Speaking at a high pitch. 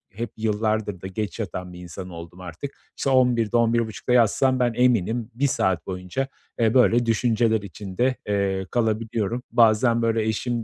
No: low, 110 Hz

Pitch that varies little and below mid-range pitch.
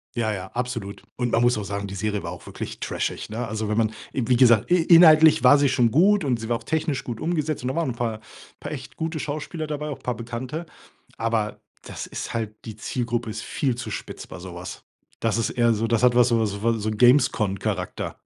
No: average, 4.2 semitones; low, 120 Hz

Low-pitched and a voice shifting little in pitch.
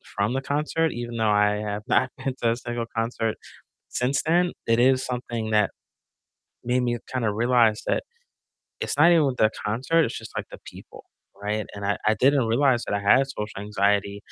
No: low, 115 Hz; average, 3.6 semitones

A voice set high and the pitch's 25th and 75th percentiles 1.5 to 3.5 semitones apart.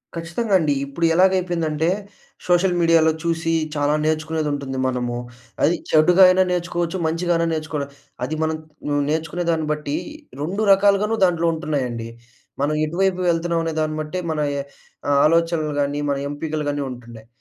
No: medium, 160 Hz; average, 2.8 semitones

